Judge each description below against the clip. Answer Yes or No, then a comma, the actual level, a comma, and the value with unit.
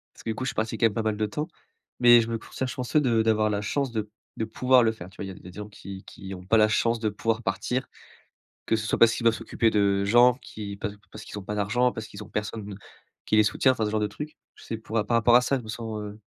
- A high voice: No, low, 110 Hz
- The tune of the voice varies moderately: No, narrow, 2.2 semitones